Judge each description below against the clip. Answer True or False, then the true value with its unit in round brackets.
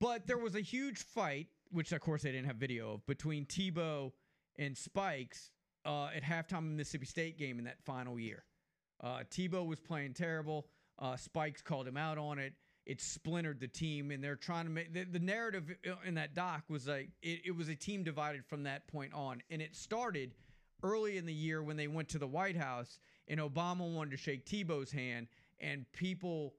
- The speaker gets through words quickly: True (210 wpm)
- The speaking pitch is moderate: True (155 Hz)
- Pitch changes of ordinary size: True (3.7 semitones)